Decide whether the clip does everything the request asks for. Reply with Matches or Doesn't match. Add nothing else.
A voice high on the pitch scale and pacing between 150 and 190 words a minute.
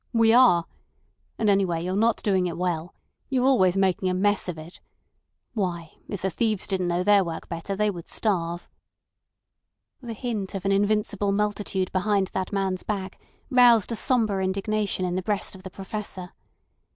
Matches